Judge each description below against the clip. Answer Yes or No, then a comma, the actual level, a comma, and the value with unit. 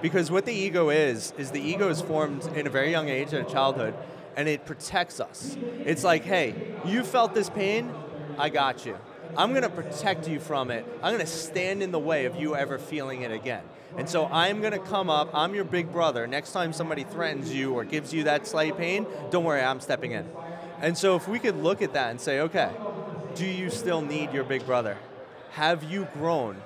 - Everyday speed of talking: No, fast, 220 wpm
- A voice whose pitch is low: No, medium, 160 Hz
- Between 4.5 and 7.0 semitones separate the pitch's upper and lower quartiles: No, average, 4.0 semitones